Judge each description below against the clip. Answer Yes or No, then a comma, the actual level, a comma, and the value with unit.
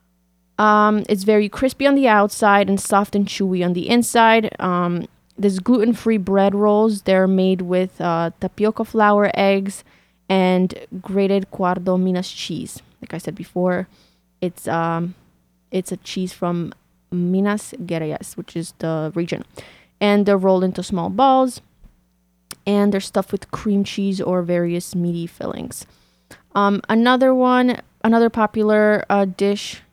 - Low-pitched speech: No, high, 195 Hz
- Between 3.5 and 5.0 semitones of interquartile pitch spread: No, average, 3.1 semitones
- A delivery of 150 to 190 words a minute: No, average, 140 wpm